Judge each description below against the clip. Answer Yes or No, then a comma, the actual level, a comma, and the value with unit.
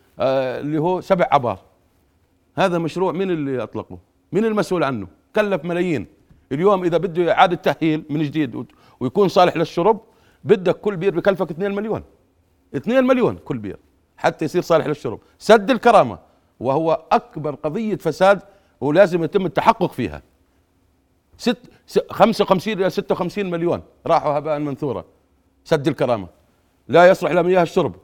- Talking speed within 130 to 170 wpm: Yes, fast, 135 wpm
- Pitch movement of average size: No, wide, 6.4 semitones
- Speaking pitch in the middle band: Yes, medium, 170 Hz